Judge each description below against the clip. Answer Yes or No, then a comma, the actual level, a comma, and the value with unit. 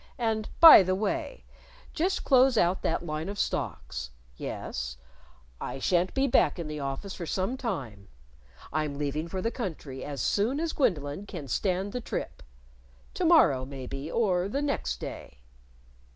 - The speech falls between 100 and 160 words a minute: Yes, average, 155 wpm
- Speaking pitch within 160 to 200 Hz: Yes, medium, 185 Hz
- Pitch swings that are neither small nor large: No, wide, 8.6 semitones